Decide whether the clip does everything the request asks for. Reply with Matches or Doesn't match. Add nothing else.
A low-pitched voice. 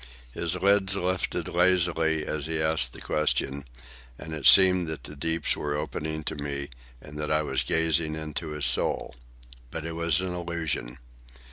Matches